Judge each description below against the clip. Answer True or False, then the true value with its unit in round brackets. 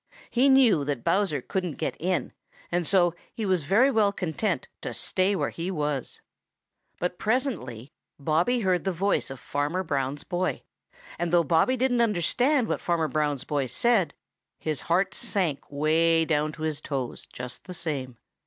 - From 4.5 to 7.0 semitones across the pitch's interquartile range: True (5.1 semitones)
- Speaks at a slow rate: False (160 wpm)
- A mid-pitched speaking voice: True (170 Hz)